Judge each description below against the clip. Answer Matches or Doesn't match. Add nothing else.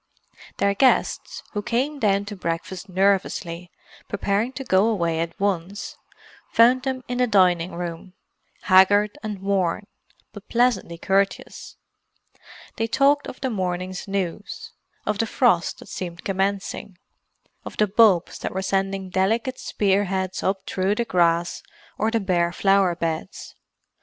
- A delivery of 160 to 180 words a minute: Doesn't match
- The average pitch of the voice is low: Doesn't match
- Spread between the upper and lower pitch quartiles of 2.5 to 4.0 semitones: Matches